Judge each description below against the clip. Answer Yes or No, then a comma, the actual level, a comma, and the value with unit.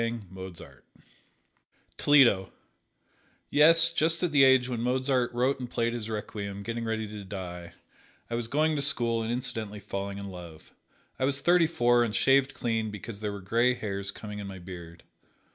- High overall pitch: No, low, 115 Hz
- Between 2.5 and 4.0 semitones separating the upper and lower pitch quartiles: No, average, 4.6 semitones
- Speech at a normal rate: Yes, average, 165 wpm